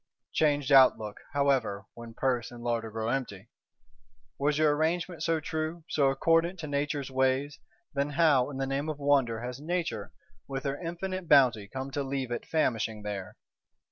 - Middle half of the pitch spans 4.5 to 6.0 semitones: No, average, 4.1 semitones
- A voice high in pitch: No, medium, 140 Hz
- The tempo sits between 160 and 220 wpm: Yes, average, 165 wpm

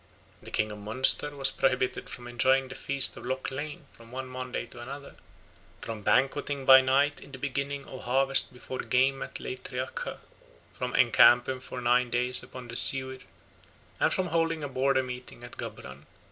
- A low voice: Yes, low, 130 Hz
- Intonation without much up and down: Yes, narrow, 1.6 semitones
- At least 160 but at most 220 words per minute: Yes, average, 175 wpm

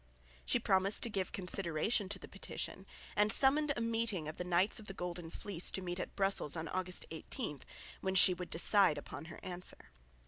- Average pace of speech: Yes, average, 195 wpm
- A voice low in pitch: No, medium, 185 Hz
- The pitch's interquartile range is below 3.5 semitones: Yes, average, 2.9 semitones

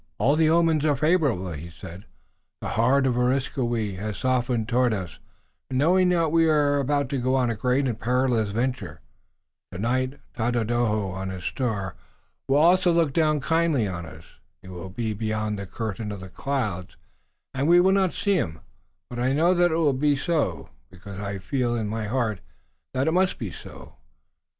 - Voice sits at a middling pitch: No, low, 125 Hz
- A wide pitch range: Yes, wide, 6.0 semitones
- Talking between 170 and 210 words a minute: Yes, average, 180 wpm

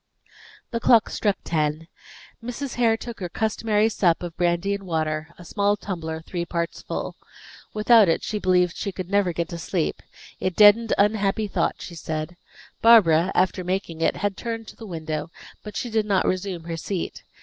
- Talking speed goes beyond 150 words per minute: Yes, average, 185 wpm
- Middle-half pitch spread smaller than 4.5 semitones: Yes, average, 4.0 semitones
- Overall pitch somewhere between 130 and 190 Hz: Yes, medium, 185 Hz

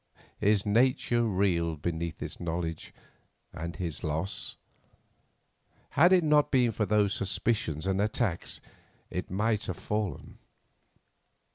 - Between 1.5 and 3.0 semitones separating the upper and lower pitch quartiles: No, average, 4.9 semitones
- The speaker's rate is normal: No, slow, 115 wpm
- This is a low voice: Yes, low, 100 Hz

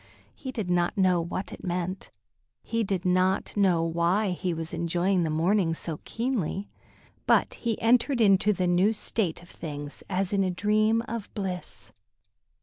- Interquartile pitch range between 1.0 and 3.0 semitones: No, average, 3.4 semitones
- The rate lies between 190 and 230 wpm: No, average, 160 wpm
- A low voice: No, medium, 185 Hz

